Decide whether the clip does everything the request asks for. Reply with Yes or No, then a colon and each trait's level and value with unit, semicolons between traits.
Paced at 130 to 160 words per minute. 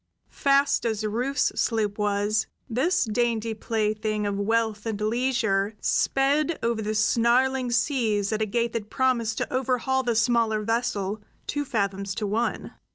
Yes: average, 145 wpm